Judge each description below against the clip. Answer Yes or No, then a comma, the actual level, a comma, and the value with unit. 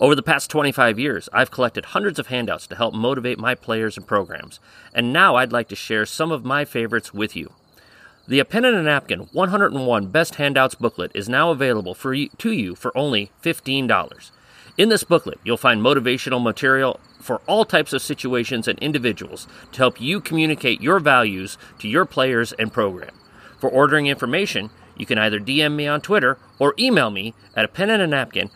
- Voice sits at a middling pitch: No, low, 130 Hz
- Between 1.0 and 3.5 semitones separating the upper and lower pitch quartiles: No, average, 4.8 semitones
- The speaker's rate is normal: Yes, average, 195 wpm